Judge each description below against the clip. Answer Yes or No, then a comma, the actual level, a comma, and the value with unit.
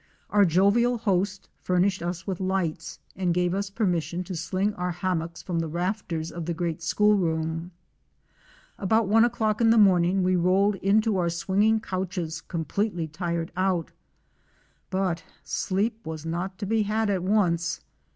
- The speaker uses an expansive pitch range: No, average, 2.9 semitones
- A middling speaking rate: Yes, average, 155 wpm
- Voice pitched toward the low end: No, medium, 185 Hz